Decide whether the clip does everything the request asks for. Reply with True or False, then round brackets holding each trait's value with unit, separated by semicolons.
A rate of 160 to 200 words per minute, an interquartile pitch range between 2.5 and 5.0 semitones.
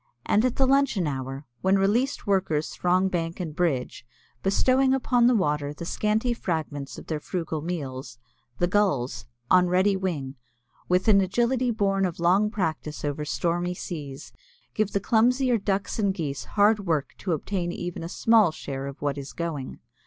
False (165 wpm; 5.5 semitones)